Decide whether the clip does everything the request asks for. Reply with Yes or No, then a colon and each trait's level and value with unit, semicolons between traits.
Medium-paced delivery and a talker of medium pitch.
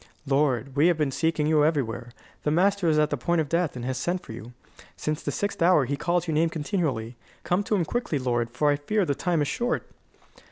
No: fast, 235 wpm; medium, 150 Hz